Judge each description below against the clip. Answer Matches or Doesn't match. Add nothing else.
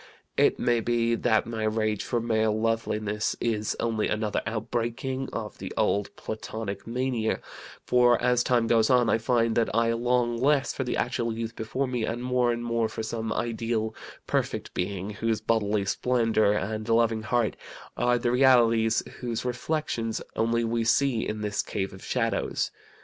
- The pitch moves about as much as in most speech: Doesn't match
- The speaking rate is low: Doesn't match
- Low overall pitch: Matches